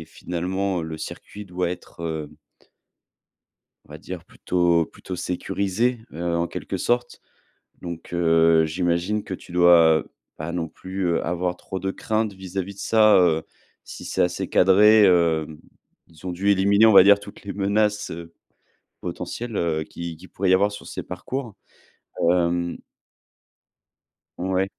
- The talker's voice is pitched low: Yes, very low, 90 Hz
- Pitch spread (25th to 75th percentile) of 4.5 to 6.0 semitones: No, average, 2.8 semitones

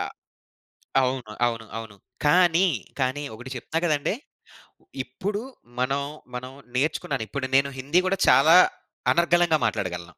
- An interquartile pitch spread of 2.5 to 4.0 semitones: No, average, 4.9 semitones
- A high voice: No, medium, 140 Hz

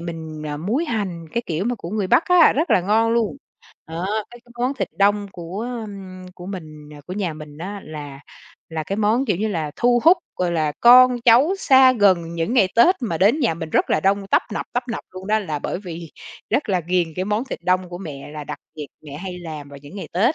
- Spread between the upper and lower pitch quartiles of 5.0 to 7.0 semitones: Yes, wide, 5.6 semitones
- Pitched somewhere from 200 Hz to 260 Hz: No, high, 190 Hz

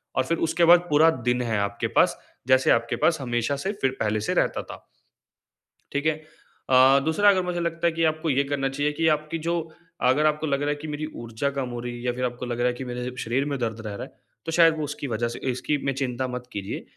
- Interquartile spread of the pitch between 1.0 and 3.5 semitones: No, average, 4.0 semitones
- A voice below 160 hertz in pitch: Yes, low, 135 Hz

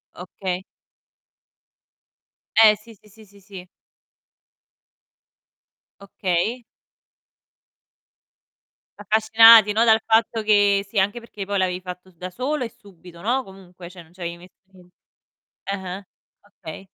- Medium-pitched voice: No, high, 195 Hz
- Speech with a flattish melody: No, average, 3.2 semitones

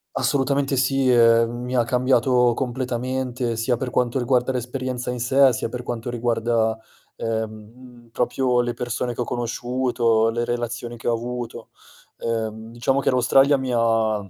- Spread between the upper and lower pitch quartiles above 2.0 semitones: No, narrow, 1.6 semitones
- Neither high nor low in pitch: No, low, 120 Hz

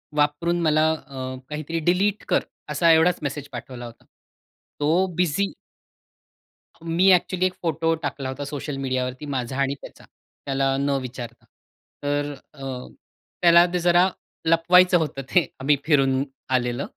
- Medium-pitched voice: Yes, medium, 145 Hz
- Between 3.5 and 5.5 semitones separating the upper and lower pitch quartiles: Yes, average, 4.0 semitones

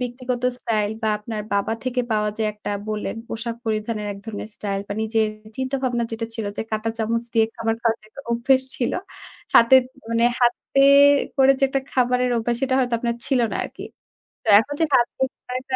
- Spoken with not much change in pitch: Yes, narrow, 2.3 semitones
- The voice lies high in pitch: Yes, high, 230 Hz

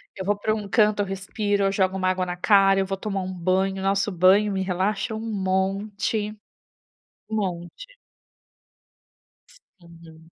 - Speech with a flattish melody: Yes, narrow, 1.8 semitones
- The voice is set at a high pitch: Yes, high, 195 Hz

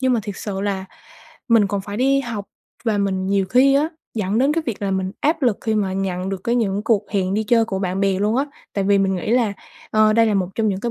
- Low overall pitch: No, high, 205 Hz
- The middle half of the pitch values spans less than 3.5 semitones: Yes, average, 3.1 semitones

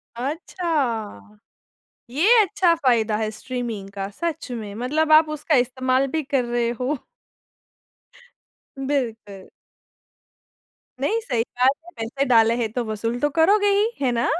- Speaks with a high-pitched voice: Yes, very high, 255 Hz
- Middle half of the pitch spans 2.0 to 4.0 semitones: No, average, 5.2 semitones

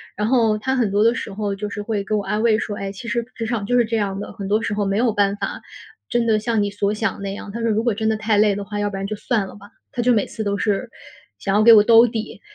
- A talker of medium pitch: No, high, 215 Hz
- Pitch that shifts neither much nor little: No, narrow, 2.0 semitones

